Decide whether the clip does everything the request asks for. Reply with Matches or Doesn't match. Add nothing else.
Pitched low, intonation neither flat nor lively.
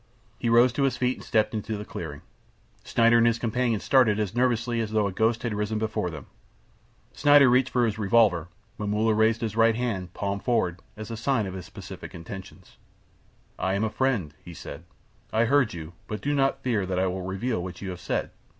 Matches